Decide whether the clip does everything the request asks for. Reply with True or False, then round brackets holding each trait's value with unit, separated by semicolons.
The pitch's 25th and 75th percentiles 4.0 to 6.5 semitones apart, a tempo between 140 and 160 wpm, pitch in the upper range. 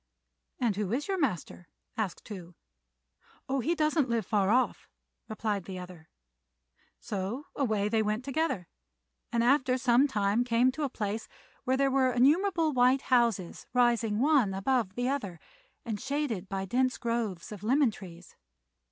True (4.8 semitones; 150 wpm; 235 Hz)